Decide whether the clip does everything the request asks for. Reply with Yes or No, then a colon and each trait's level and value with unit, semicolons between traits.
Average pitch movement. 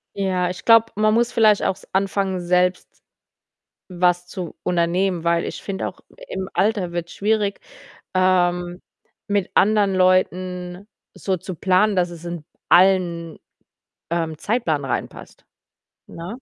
No: narrow, 2.2 semitones